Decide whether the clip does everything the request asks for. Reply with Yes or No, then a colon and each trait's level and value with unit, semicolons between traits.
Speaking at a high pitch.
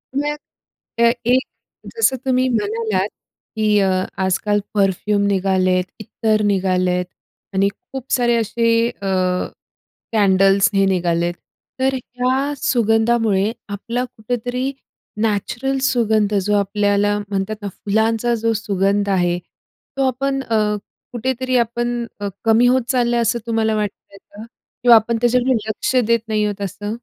Yes: high, 220 Hz